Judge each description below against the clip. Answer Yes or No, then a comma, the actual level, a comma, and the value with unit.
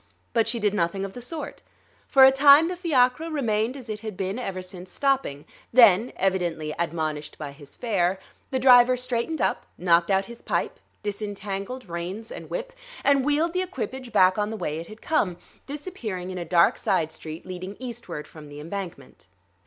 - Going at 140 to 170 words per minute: No, average, 185 wpm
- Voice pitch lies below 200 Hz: No, high, 210 Hz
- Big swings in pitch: Yes, wide, 6.3 semitones